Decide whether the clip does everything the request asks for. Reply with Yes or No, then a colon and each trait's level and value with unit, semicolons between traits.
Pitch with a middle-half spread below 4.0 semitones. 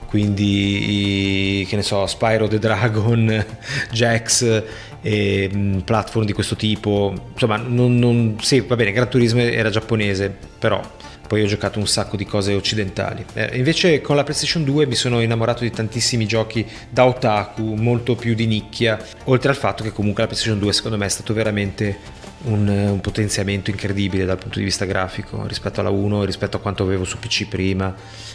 Yes: narrow, 2.4 semitones